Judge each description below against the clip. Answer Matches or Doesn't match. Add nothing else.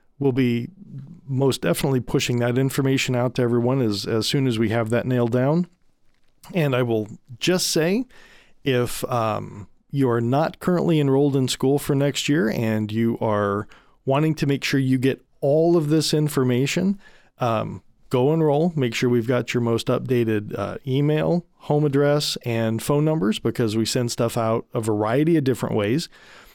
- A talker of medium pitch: Doesn't match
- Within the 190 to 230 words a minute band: Doesn't match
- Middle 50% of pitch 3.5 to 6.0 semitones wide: Matches